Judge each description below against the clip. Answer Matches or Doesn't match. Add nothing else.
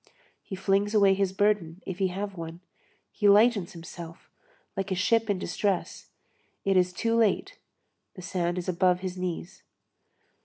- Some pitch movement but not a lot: Doesn't match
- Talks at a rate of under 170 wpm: Matches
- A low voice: Doesn't match